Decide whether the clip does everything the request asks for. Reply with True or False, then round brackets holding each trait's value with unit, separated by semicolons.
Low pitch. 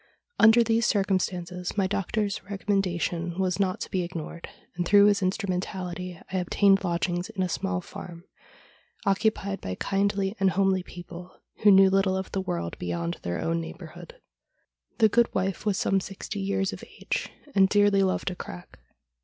False (190 Hz)